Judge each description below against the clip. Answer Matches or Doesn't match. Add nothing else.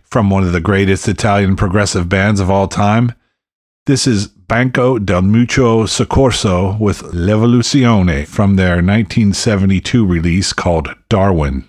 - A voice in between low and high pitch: Doesn't match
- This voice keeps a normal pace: Doesn't match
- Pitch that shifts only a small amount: Doesn't match